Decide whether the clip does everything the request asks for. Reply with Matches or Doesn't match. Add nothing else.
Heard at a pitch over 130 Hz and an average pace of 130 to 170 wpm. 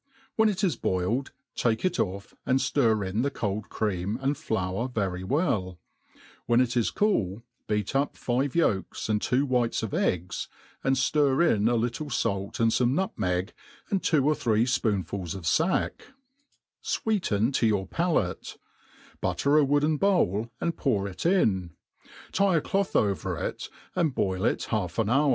Doesn't match